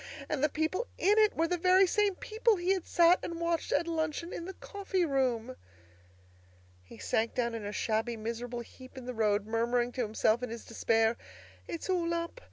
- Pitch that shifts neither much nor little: No, wide, 7.4 semitones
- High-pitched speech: Yes, very high, 270 Hz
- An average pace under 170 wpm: No, average, 195 wpm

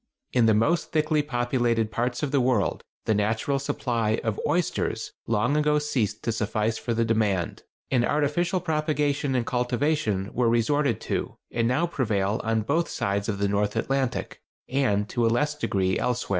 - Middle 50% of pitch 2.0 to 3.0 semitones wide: No, average, 5.0 semitones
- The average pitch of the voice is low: Yes, low, 120 Hz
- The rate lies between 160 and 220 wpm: Yes, average, 170 wpm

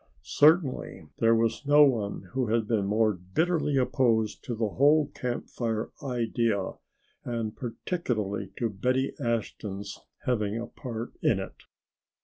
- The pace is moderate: No, slow, 130 wpm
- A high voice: No, low, 115 Hz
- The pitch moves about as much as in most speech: Yes, average, 3.4 semitones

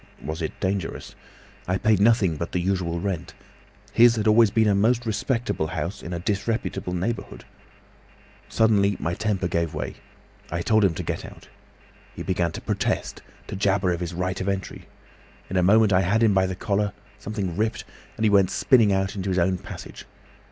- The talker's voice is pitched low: Yes, very low, 95 Hz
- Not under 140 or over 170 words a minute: No, average, 185 wpm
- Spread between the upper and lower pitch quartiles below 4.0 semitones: Yes, average, 3.2 semitones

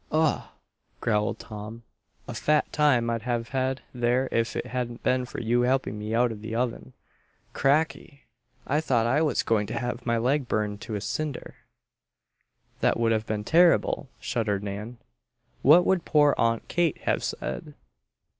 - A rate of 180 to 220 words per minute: No, average, 165 wpm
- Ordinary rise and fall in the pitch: Yes, average, 3.7 semitones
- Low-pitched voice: Yes, low, 120 Hz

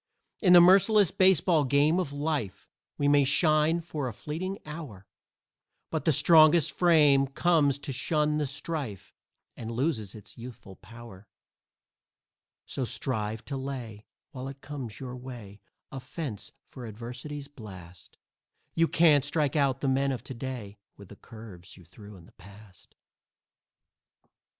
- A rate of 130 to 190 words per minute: Yes, average, 145 wpm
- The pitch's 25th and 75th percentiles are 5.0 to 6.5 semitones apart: Yes, wide, 5.4 semitones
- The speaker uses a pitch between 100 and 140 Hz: Yes, low, 135 Hz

